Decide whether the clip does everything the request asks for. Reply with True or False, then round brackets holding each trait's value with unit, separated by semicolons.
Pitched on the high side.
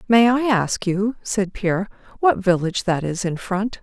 True (200 Hz)